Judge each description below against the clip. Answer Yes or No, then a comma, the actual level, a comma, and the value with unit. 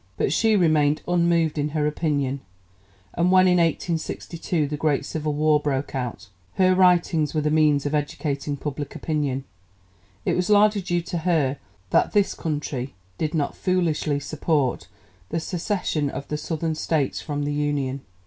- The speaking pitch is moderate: Yes, medium, 155 Hz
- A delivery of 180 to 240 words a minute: No, average, 160 wpm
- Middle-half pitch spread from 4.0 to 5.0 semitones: No, average, 2.9 semitones